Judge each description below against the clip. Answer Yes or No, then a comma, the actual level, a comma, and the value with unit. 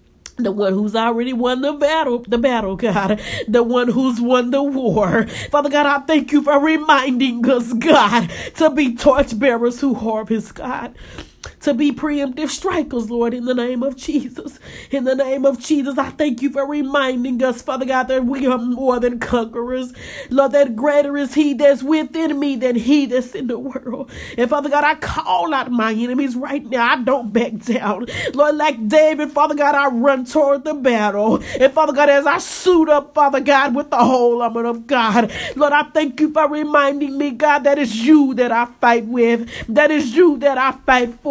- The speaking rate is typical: Yes, average, 195 wpm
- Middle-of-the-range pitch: No, very high, 270 Hz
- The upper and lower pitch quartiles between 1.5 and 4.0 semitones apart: Yes, average, 3.2 semitones